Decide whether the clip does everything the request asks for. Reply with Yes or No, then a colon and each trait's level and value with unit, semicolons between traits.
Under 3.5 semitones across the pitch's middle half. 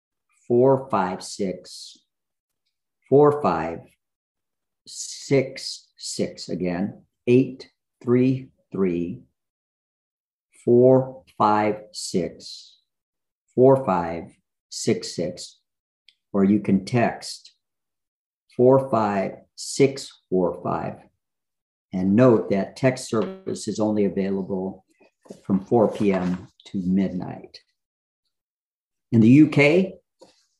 No: average, 5.3 semitones